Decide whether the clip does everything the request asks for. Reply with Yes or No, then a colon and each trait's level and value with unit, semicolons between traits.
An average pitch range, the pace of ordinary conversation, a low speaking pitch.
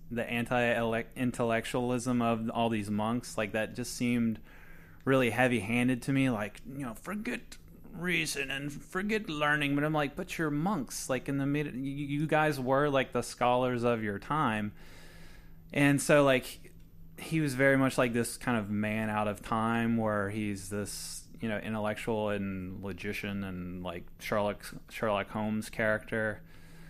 Yes: average, 4.5 semitones; average, 160 wpm; low, 120 Hz